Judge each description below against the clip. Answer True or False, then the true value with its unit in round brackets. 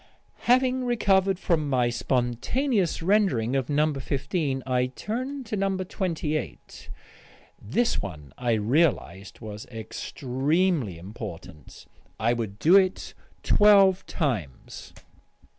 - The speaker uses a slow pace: True (105 wpm)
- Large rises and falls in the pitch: True (8.7 semitones)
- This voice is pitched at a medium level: True (145 Hz)